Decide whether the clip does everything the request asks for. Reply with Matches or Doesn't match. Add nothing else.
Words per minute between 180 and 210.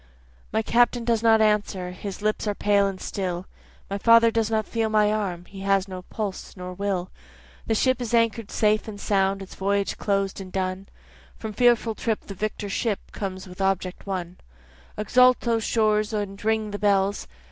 Matches